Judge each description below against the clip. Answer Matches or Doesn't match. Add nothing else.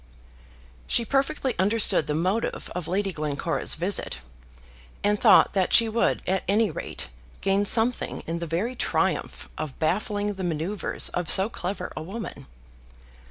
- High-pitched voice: Matches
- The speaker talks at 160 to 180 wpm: Doesn't match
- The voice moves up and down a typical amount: Matches